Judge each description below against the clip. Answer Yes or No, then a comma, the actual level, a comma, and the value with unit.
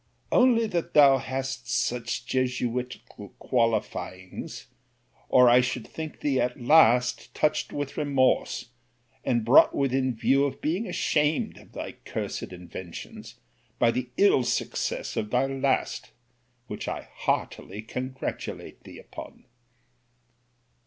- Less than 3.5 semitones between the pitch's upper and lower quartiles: Yes, average, 2.8 semitones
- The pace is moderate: No, slow, 120 wpm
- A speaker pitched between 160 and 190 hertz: No, low, 130 Hz